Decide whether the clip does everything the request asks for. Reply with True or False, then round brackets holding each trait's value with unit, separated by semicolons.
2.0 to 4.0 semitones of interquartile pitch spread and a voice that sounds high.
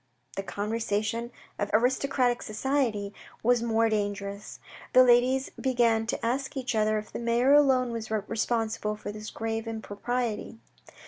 True (2.6 semitones; 225 Hz)